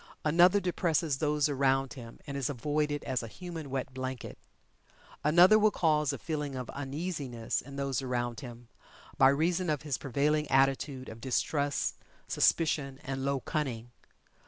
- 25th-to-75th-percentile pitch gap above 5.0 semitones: No, average, 2.7 semitones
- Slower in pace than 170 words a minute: Yes, average, 150 wpm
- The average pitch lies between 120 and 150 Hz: Yes, medium, 140 Hz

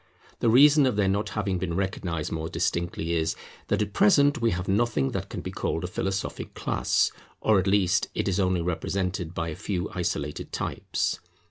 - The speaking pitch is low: Yes, very low, 95 Hz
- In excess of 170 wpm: Yes, average, 190 wpm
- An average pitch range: Yes, average, 3.3 semitones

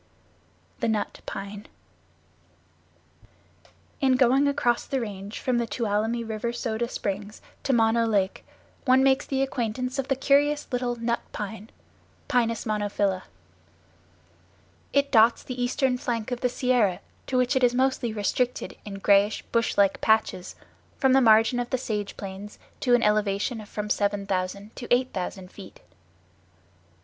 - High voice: Yes, high, 230 Hz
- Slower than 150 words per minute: Yes, average, 140 wpm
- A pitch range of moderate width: Yes, average, 3.5 semitones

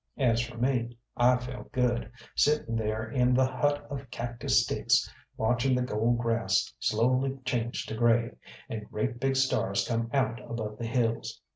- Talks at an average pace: Yes, average, 160 wpm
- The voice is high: No, low, 120 Hz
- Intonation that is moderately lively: No, narrow, 2.0 semitones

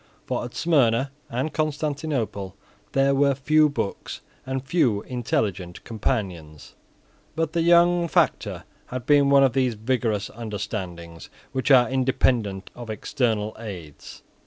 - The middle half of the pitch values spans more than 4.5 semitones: Yes, average, 5.2 semitones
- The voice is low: Yes, low, 125 Hz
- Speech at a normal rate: No, slow, 120 wpm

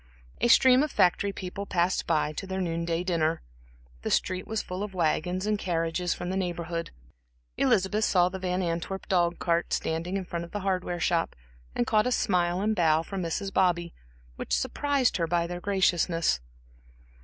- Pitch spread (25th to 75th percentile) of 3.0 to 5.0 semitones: No, narrow, 2.4 semitones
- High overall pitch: No, medium, 180 Hz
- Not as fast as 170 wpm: No, average, 180 wpm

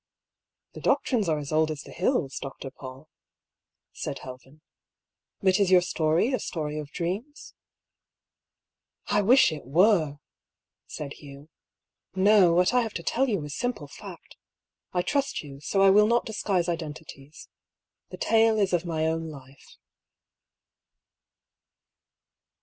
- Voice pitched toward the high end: No, medium, 170 Hz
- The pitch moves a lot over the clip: Yes, wide, 5.7 semitones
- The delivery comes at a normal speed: Yes, average, 155 wpm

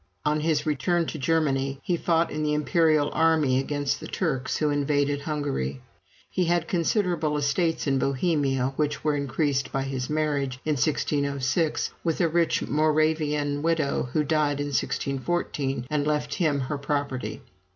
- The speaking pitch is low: No, medium, 150 Hz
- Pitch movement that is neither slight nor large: No, narrow, 2.3 semitones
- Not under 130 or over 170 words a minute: Yes, average, 150 wpm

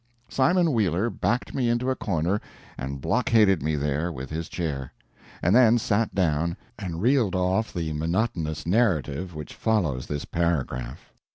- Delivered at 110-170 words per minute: Yes, average, 150 wpm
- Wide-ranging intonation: Yes, wide, 6.3 semitones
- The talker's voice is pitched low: Yes, very low, 90 Hz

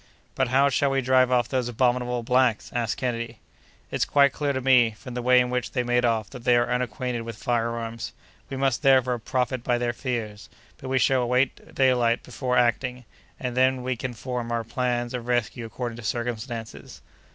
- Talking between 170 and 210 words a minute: Yes, average, 195 wpm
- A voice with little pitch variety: Yes, narrow, 1.5 semitones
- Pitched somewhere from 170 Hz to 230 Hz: No, low, 125 Hz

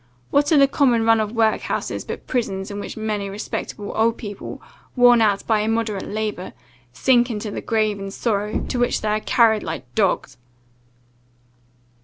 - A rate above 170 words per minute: No, average, 165 wpm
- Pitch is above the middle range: Yes, high, 215 Hz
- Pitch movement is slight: Yes, narrow, 2.2 semitones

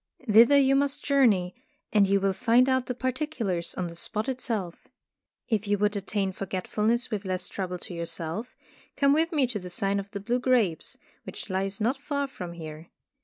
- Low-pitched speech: No, high, 210 Hz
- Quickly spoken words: No, average, 185 wpm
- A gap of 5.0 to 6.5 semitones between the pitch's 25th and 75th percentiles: Yes, average, 5.3 semitones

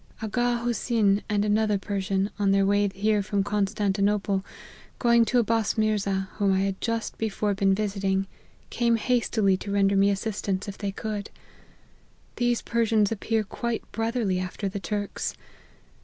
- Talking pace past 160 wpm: No, average, 150 wpm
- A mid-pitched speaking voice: No, high, 205 Hz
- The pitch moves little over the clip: Yes, narrow, 2.2 semitones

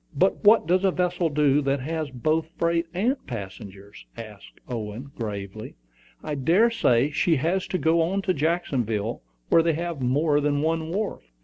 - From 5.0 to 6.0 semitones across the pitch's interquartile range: Yes, wide, 5.6 semitones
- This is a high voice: No, medium, 155 Hz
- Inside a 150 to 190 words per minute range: Yes, average, 165 wpm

